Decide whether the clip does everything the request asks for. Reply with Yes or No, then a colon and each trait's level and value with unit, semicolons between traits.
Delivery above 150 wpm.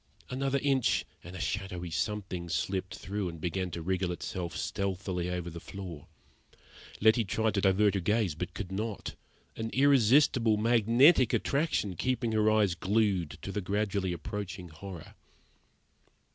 No: average, 145 wpm